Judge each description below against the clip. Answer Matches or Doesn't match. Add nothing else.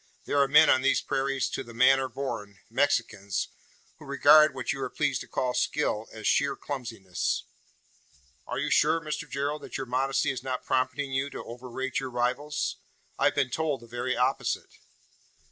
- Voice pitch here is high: Doesn't match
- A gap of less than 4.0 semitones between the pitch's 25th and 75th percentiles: Matches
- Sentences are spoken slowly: Doesn't match